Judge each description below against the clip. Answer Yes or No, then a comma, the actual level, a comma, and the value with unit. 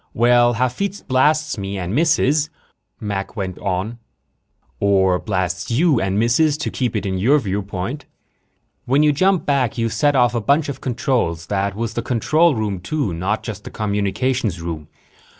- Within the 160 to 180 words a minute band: Yes, average, 170 wpm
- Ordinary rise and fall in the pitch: No, wide, 6.1 semitones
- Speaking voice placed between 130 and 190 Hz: No, low, 115 Hz